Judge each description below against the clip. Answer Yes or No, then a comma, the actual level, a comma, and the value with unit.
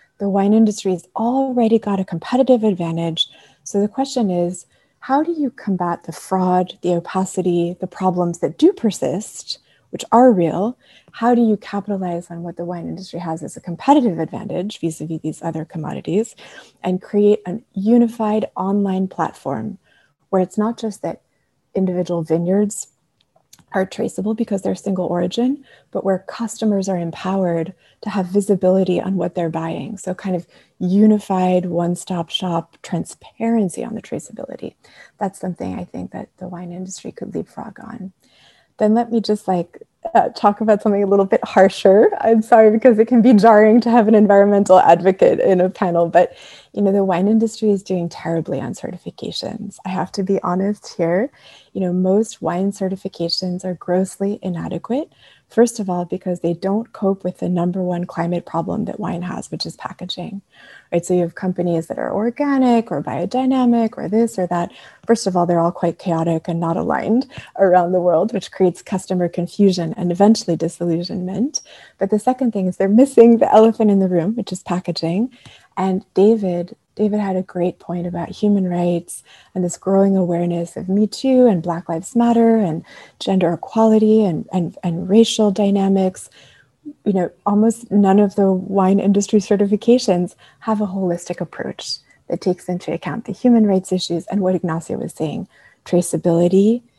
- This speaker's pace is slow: No, average, 175 wpm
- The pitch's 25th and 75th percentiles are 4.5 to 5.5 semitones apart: No, average, 3.6 semitones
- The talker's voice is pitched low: No, high, 190 Hz